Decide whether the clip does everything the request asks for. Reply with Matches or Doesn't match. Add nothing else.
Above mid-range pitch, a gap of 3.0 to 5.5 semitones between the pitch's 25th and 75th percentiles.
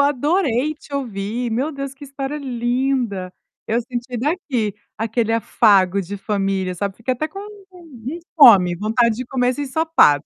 Matches